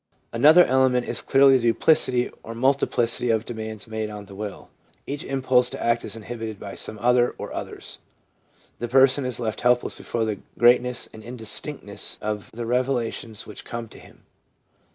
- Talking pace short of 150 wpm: No, average, 175 wpm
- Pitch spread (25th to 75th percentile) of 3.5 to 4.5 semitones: No, narrow, 2.5 semitones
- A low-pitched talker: Yes, low, 120 Hz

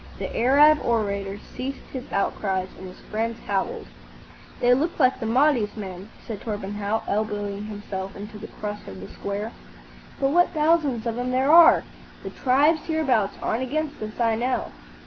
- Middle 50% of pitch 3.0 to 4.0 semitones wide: No, average, 4.7 semitones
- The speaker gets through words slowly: No, average, 165 wpm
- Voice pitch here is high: Yes, high, 225 Hz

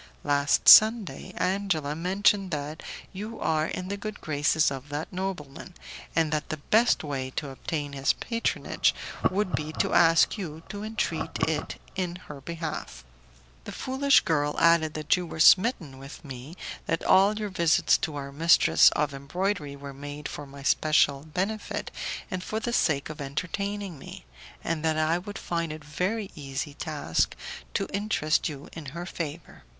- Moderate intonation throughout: Yes, average, 4.7 semitones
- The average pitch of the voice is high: No, medium, 160 Hz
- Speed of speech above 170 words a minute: No, average, 165 wpm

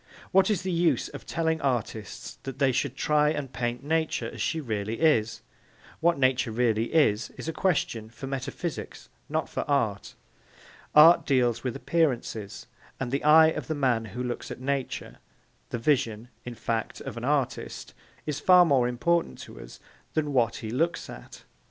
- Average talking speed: Yes, average, 170 wpm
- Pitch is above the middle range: No, low, 135 Hz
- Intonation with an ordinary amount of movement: Yes, average, 5.0 semitones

